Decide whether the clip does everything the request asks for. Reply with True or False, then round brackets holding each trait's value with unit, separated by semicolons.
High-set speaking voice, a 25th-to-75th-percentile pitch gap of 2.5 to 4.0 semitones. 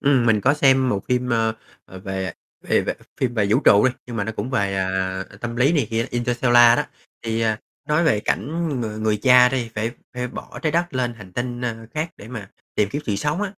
False (120 Hz; 3.4 semitones)